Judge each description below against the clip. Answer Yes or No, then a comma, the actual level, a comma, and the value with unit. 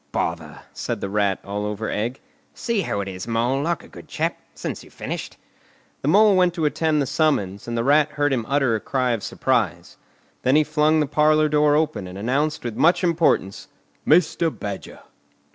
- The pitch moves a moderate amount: No, wide, 6.6 semitones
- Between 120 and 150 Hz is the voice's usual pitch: Yes, medium, 140 Hz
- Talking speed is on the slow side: No, average, 195 wpm